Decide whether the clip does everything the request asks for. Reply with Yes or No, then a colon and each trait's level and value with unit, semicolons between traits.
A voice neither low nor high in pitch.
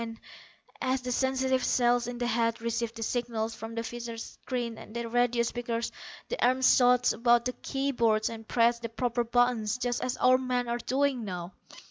No: high, 240 Hz